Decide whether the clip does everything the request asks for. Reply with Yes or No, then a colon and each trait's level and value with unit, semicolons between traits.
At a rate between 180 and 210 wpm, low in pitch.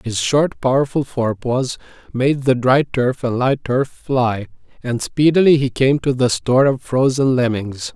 No: average, 165 wpm; low, 130 Hz